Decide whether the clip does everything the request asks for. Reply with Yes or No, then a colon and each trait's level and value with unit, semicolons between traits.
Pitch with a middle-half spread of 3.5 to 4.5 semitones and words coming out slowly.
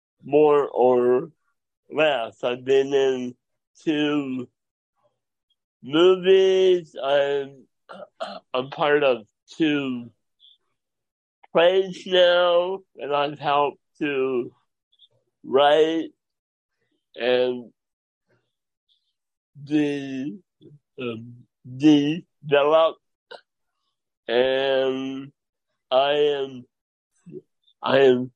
Yes: average, 4.0 semitones; slow, 65 wpm